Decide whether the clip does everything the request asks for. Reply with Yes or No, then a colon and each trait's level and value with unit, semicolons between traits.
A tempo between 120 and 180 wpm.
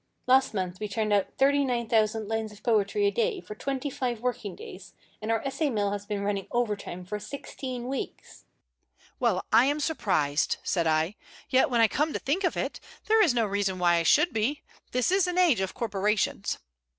No: average, 200 wpm